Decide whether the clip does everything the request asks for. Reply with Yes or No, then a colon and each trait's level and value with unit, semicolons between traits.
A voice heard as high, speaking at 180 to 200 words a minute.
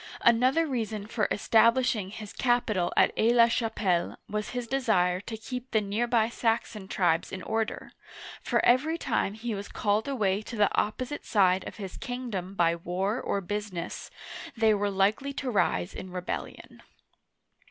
No: high, 215 Hz; average, 160 wpm